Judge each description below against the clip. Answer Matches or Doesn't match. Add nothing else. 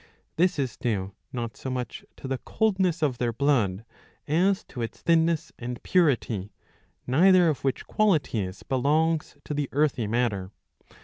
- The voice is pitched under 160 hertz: Matches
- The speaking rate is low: Doesn't match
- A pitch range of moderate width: Doesn't match